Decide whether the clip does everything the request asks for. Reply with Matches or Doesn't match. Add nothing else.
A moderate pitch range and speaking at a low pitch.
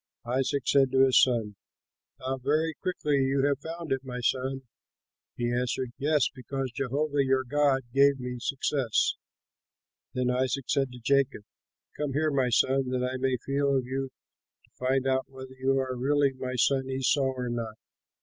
Doesn't match